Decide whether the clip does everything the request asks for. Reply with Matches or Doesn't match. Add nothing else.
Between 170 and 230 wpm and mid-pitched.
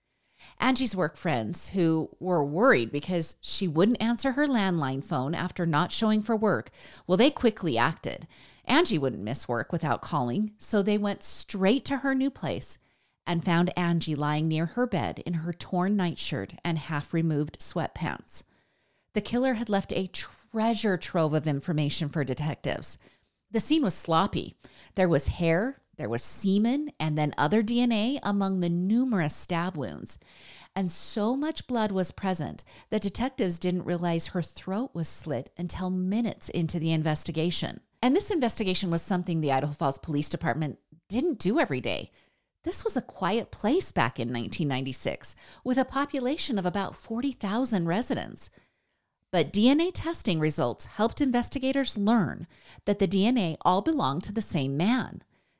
Doesn't match